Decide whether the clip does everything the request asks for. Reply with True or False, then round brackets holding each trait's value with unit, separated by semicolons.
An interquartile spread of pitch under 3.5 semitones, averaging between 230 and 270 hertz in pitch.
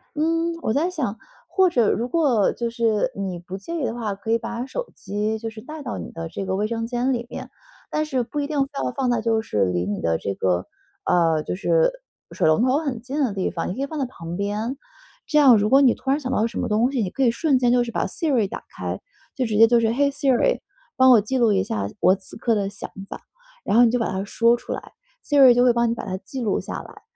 False (4.8 semitones; 235 Hz)